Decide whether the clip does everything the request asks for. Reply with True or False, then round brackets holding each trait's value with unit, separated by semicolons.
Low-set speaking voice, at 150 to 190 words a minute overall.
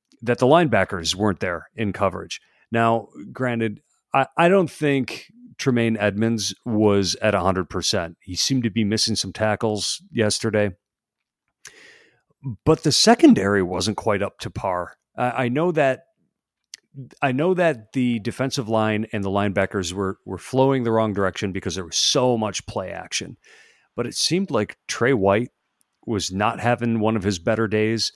True (110 Hz; 160 wpm)